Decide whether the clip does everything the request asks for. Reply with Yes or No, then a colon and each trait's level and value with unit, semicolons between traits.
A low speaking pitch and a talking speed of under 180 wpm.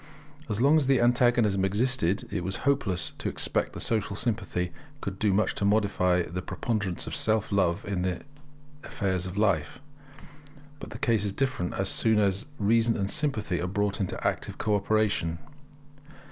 Yes: low, 100 Hz; average, 170 wpm